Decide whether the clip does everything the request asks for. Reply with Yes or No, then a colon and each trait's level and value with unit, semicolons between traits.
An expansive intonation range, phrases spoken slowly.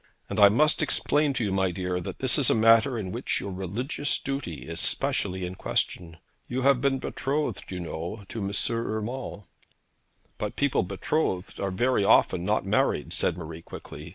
No: wide, 6.2 semitones; average, 180 wpm